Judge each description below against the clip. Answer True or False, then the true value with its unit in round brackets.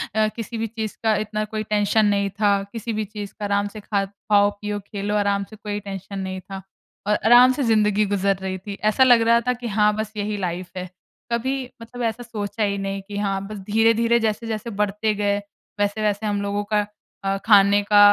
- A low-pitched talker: False (210 Hz)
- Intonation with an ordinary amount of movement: False (1.6 semitones)